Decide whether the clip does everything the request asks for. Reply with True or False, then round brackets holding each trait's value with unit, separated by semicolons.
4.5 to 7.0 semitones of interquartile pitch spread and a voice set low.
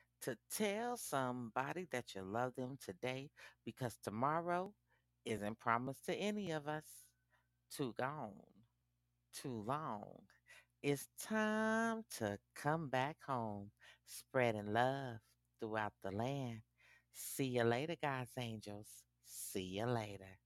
True (5.1 semitones; 120 Hz)